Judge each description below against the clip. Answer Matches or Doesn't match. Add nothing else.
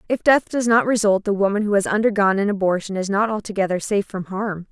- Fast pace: Matches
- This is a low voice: Doesn't match